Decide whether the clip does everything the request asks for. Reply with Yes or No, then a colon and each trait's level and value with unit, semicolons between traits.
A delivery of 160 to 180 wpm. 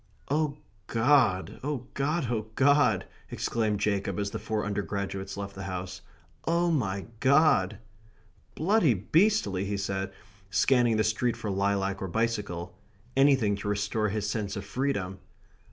No: slow, 135 wpm